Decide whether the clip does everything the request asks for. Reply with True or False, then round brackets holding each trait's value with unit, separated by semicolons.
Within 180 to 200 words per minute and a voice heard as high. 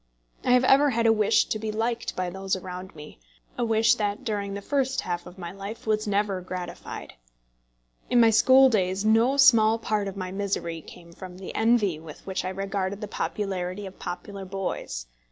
True (190 wpm; 200 Hz)